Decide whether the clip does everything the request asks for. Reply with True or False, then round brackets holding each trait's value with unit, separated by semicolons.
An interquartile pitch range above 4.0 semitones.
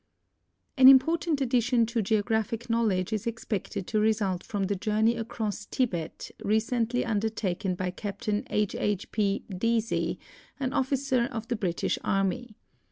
False (2.8 semitones)